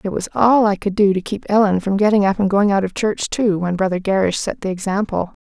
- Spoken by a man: No, female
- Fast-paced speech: Yes, fast, 265 wpm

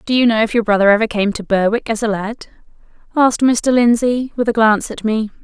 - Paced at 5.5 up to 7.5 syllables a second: Yes, 6.0 syllables/s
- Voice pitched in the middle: No, high, 225 Hz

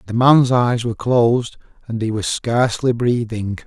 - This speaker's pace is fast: No, average, 165 wpm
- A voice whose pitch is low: Yes, low, 120 Hz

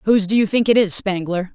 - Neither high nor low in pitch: No, high, 200 Hz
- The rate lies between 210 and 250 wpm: No, fast, 270 wpm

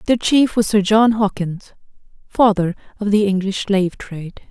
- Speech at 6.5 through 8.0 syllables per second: No, 4.7 syllables/s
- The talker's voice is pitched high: Yes, high, 205 Hz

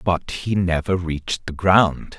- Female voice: No, male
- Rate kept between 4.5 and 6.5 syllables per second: No, 3.9 syllables/s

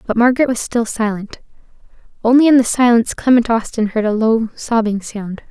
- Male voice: No, female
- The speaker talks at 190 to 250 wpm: No, average, 175 wpm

